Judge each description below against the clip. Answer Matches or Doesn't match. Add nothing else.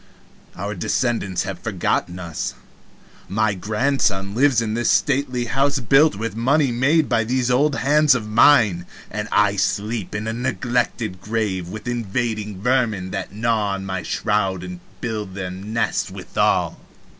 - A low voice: Matches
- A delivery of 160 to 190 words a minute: Doesn't match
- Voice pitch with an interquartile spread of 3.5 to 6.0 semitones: Matches